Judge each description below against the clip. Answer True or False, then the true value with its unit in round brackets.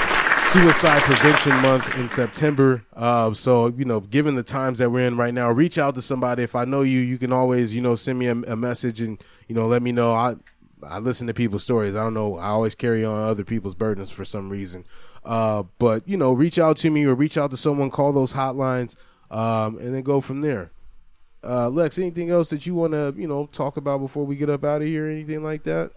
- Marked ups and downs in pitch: False (4.0 semitones)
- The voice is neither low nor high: False (125 Hz)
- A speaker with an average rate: False (245 wpm)